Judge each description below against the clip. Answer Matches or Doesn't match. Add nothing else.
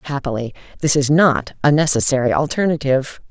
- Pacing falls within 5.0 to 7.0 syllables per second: Matches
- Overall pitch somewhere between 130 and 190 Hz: Matches